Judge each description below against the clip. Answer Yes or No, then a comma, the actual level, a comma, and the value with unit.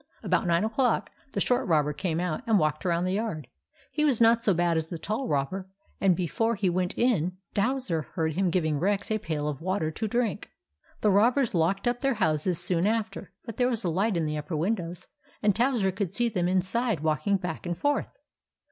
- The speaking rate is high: Yes, fast, 210 wpm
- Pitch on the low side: No, high, 190 Hz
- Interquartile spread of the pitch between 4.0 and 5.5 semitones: Yes, average, 5.2 semitones